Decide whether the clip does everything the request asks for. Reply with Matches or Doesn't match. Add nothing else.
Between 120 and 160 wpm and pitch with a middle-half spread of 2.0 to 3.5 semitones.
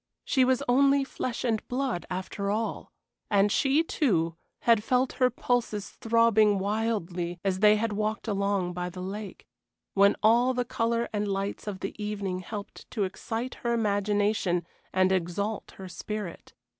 Matches